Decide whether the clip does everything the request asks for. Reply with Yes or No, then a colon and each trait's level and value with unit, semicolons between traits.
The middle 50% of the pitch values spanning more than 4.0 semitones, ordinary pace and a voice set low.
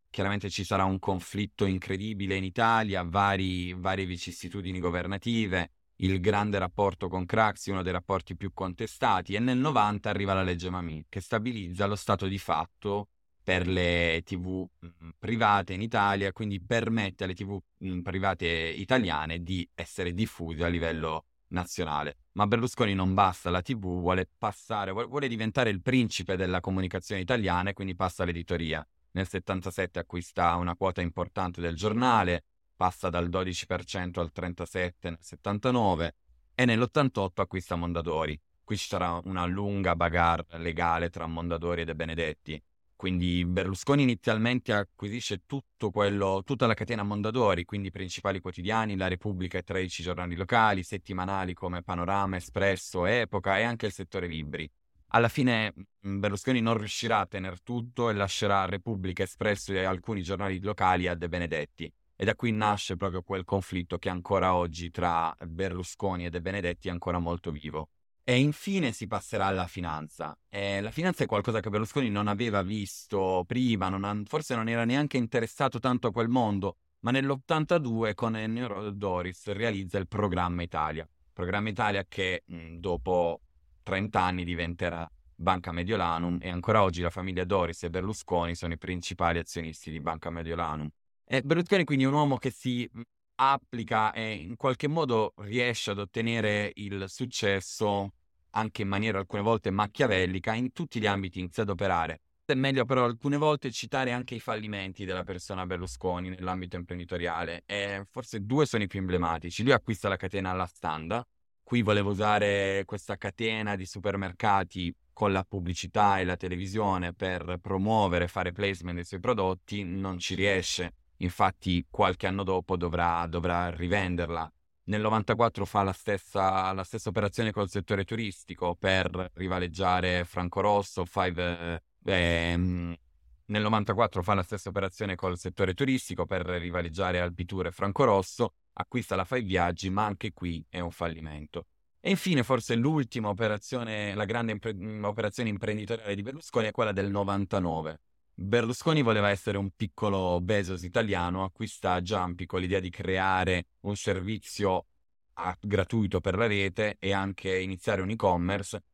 No: average, 3.2 semitones; average, 155 wpm; very low, 95 Hz